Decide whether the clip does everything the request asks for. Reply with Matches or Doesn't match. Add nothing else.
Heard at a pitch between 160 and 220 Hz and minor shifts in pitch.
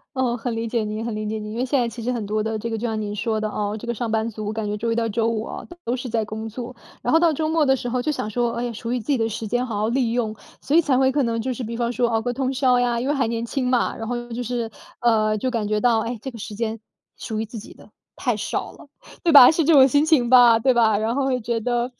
Doesn't match